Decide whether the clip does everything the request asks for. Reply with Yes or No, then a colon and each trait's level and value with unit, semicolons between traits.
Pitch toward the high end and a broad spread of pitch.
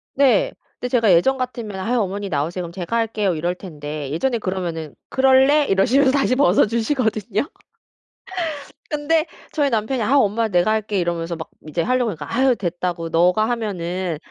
Yes: high, 210 Hz; wide, 6.4 semitones